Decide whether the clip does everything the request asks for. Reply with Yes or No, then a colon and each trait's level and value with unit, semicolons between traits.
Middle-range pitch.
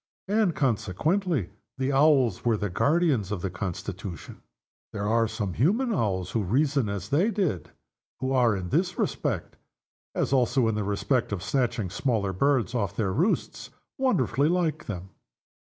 No: low, 120 Hz